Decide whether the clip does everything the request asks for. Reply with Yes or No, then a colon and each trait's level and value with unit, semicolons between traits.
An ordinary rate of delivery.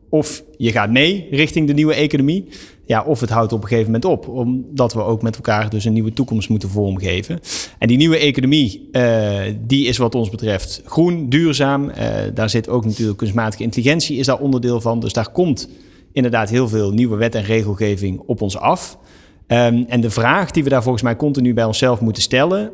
No: fast, 205 wpm